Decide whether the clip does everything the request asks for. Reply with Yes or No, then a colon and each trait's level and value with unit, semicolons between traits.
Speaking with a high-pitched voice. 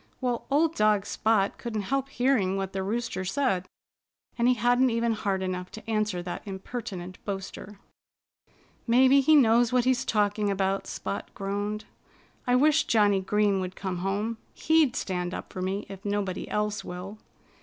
Yes: high, 210 Hz